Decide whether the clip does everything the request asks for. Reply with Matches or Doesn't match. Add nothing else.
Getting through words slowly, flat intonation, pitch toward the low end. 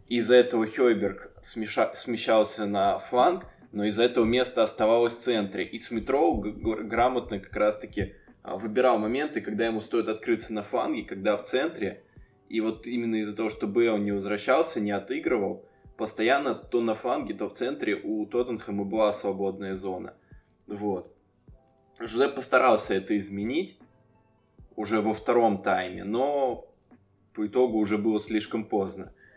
Doesn't match